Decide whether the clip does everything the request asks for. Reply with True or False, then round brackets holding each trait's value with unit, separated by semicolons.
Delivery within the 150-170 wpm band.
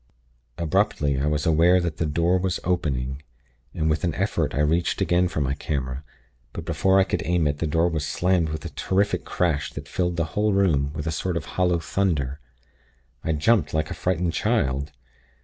False (195 wpm)